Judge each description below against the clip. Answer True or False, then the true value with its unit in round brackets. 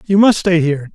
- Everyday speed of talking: False (255 wpm)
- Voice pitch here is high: False (175 Hz)